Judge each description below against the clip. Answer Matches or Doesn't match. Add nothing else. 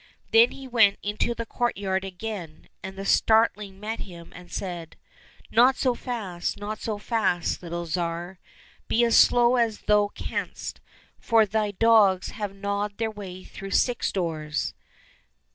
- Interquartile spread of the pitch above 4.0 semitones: Doesn't match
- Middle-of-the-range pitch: Doesn't match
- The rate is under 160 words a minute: Matches